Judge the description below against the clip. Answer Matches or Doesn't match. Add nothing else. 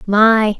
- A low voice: Doesn't match